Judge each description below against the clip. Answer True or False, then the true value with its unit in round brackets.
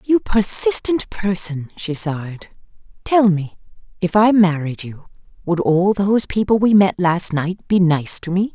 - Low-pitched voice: False (185 Hz)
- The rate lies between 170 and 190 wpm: False (160 wpm)